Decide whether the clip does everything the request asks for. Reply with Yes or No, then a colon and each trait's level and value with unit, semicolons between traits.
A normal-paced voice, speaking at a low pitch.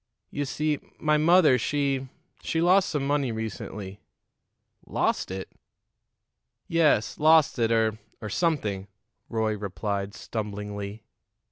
No: slow, 110 wpm; low, 115 Hz